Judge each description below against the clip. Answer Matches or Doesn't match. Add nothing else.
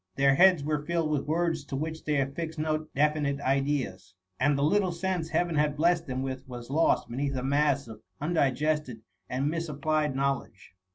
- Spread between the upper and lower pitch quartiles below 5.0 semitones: Matches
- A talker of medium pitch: Matches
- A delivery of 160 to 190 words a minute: Matches